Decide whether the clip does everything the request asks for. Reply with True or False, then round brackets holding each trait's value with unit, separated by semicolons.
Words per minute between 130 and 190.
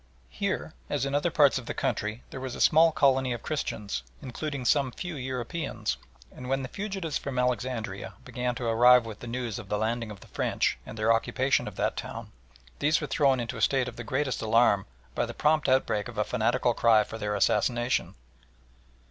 False (200 wpm)